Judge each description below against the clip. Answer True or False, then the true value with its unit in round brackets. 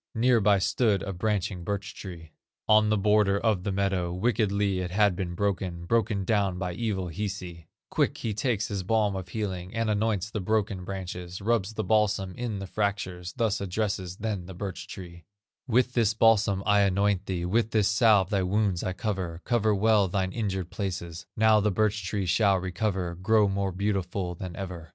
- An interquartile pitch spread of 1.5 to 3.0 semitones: True (2.7 semitones)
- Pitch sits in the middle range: False (100 Hz)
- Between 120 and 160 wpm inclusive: False (185 wpm)